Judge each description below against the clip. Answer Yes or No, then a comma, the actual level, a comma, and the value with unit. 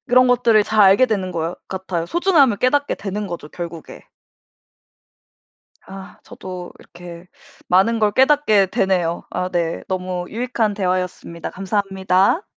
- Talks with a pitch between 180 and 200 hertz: Yes, high, 190 Hz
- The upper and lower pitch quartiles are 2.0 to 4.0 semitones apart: Yes, average, 3.6 semitones